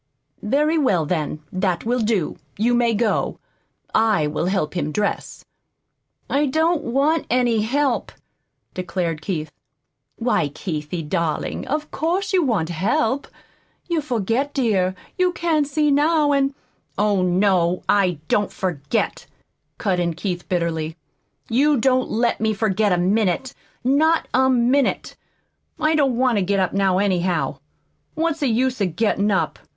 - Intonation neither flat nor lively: No, wide, 7.1 semitones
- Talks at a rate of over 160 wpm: No, average, 145 wpm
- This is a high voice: Yes, high, 220 Hz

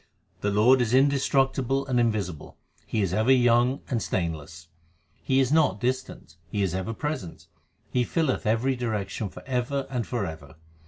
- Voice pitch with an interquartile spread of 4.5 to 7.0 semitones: Yes, average, 5.2 semitones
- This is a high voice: No, low, 120 Hz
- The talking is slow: No, average, 160 wpm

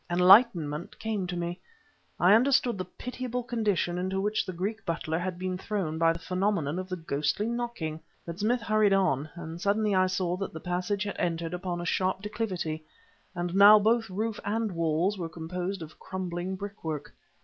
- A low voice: No, medium, 185 Hz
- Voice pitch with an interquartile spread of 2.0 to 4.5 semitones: Yes, average, 3.4 semitones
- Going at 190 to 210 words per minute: No, average, 180 wpm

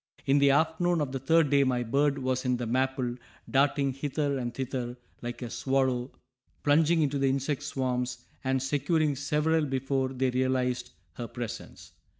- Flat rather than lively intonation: Yes, narrow, 2.2 semitones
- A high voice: No, low, 135 Hz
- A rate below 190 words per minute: Yes, average, 160 wpm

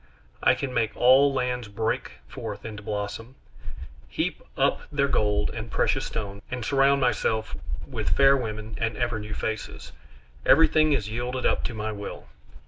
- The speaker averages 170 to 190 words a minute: No, average, 155 wpm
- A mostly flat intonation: No, average, 3.5 semitones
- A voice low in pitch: Yes, low, 115 Hz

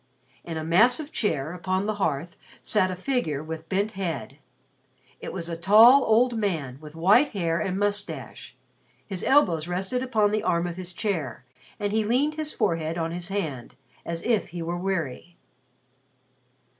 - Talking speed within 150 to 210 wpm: Yes, average, 165 wpm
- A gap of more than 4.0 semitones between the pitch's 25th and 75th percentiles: Yes, average, 4.6 semitones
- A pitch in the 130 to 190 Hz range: Yes, medium, 185 Hz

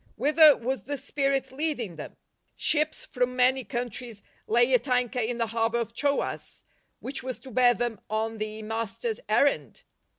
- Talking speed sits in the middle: Yes, average, 165 wpm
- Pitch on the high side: Yes, high, 245 Hz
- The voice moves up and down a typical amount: Yes, average, 3.0 semitones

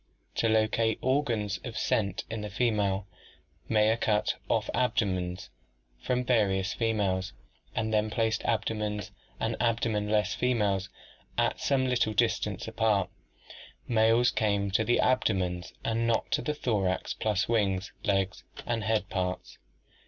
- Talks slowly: Yes, slow, 130 wpm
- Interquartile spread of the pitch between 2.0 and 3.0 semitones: Yes, average, 2.7 semitones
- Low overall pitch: Yes, low, 110 Hz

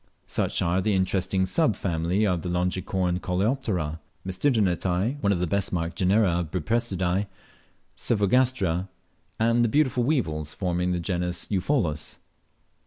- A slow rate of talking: Yes, slow, 125 wpm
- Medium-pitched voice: No, very low, 95 Hz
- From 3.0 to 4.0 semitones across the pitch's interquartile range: Yes, average, 3.7 semitones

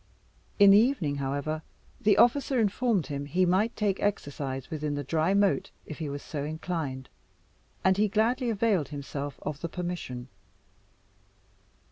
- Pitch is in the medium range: Yes, medium, 170 Hz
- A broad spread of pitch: Yes, wide, 6.1 semitones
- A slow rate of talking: No, average, 145 wpm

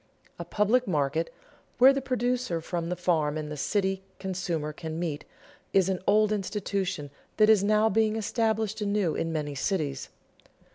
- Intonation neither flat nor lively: Yes, average, 4.9 semitones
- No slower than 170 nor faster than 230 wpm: No, average, 155 wpm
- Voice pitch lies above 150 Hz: Yes, high, 190 Hz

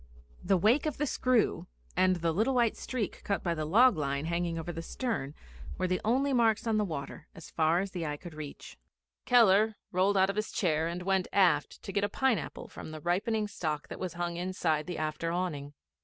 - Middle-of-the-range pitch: Yes, medium, 180 Hz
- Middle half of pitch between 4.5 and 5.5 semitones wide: Yes, average, 4.8 semitones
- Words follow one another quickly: Yes, fast, 210 wpm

